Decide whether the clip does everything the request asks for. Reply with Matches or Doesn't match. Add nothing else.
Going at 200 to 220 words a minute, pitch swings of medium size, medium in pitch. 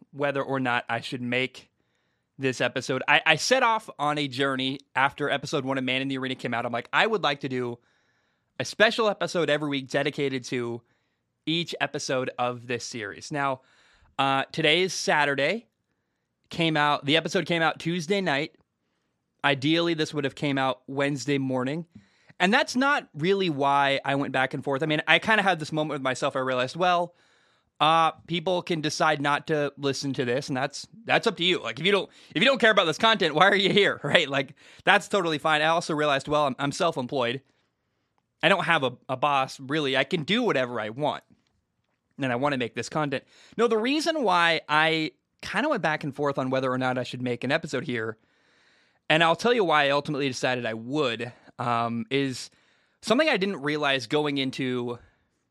Matches